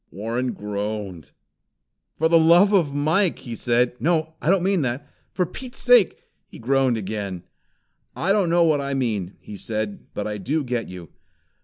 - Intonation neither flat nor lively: No, wide, 7.8 semitones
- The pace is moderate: Yes, average, 175 wpm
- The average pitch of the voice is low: Yes, low, 130 Hz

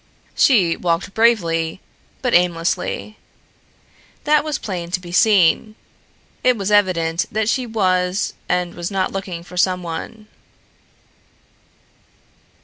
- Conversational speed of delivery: No, slow, 110 wpm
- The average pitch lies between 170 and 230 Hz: Yes, medium, 185 Hz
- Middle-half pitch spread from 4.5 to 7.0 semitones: No, average, 3.8 semitones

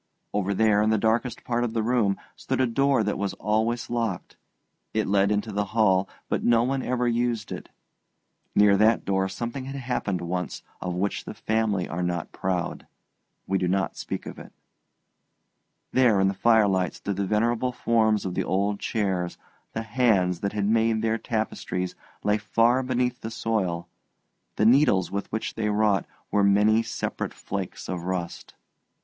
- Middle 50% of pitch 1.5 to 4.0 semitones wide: Yes, average, 3.2 semitones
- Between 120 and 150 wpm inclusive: No, average, 170 wpm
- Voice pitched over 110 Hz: No, low, 105 Hz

